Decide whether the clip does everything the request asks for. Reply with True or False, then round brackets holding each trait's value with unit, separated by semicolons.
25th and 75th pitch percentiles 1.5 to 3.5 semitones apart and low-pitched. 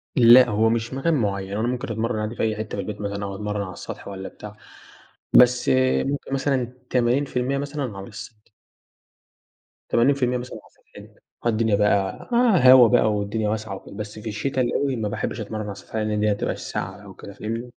True (3.2 semitones; 110 Hz)